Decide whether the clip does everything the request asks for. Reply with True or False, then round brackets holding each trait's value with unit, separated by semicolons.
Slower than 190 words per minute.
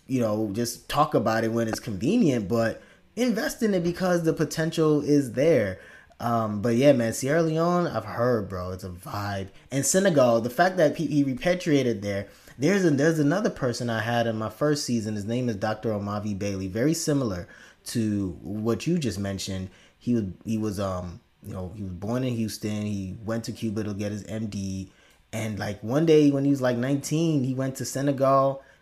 False (200 wpm)